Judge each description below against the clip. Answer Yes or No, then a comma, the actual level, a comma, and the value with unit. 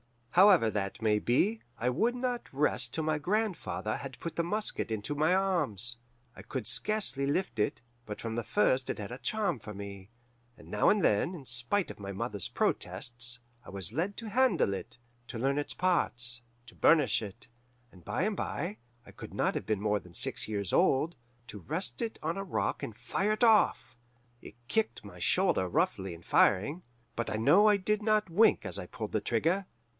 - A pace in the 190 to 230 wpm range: Yes, average, 200 wpm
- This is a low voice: Yes, low, 130 Hz